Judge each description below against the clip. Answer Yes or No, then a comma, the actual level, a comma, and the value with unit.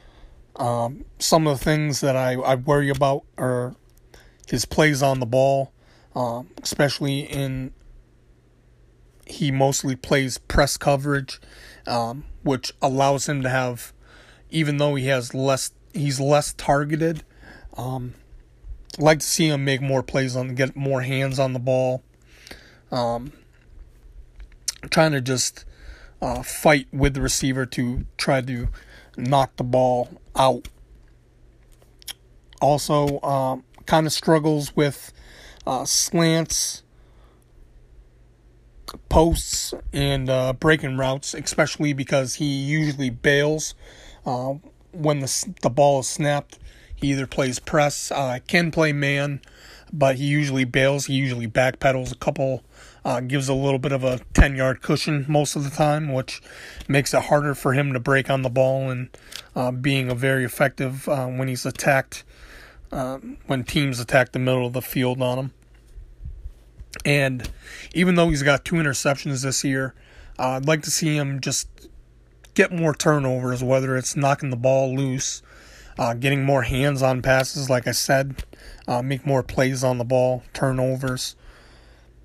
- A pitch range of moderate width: No, narrow, 2.2 semitones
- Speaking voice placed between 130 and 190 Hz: Yes, low, 135 Hz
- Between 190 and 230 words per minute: No, average, 145 wpm